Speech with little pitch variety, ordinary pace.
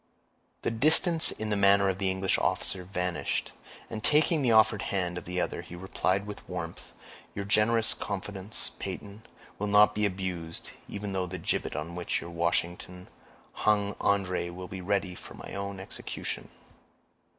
Yes: narrow, 2.3 semitones; average, 160 wpm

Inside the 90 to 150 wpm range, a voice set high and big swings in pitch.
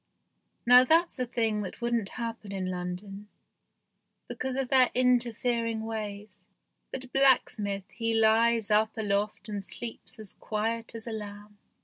No: average, 140 wpm; high, 220 Hz; narrow, 2.6 semitones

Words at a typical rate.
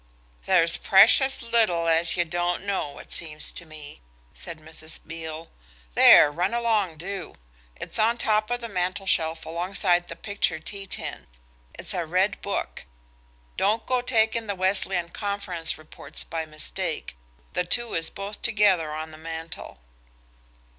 Yes: average, 145 wpm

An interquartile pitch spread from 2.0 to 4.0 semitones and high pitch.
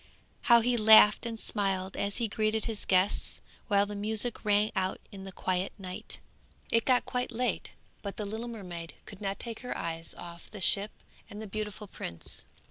Yes: narrow, 2.6 semitones; high, 210 Hz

